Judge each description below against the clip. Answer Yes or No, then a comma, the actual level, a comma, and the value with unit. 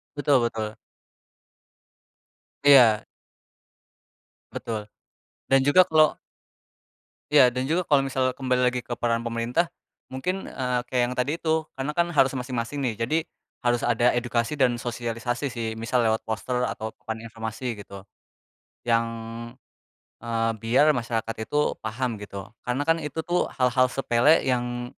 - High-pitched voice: No, low, 125 Hz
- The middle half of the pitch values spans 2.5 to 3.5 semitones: Yes, average, 3.1 semitones